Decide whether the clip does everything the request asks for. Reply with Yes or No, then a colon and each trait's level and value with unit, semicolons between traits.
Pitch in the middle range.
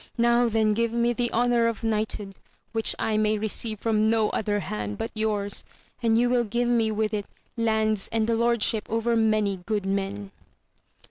No: high, 220 Hz